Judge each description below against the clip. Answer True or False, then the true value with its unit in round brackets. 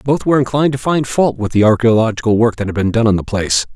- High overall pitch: False (115 Hz)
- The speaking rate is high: True (270 wpm)